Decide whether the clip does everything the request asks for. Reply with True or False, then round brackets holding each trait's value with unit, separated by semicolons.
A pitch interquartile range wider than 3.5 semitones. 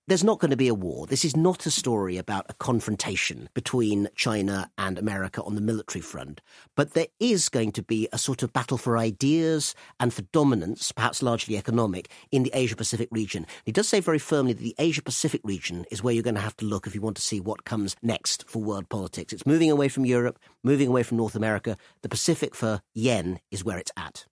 True (4.3 semitones)